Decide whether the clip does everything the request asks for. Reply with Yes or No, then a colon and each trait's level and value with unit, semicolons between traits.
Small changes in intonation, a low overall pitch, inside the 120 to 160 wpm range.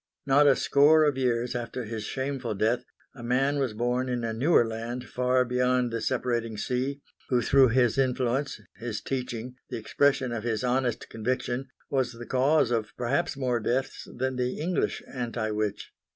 No: narrow, 2.2 semitones; low, 125 Hz; average, 170 wpm